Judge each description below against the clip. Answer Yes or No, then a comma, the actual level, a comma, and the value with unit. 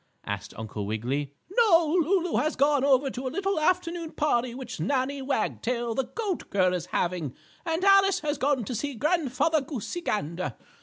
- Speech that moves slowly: No, average, 165 wpm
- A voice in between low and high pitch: No, very high, 270 Hz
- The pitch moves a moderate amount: No, wide, 8.3 semitones